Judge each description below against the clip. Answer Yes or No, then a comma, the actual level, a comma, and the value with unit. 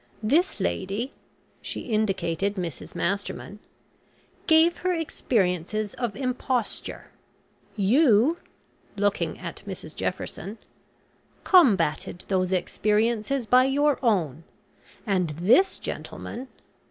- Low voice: No, high, 215 Hz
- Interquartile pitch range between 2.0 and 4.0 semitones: No, wide, 5.5 semitones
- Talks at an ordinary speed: No, slow, 90 wpm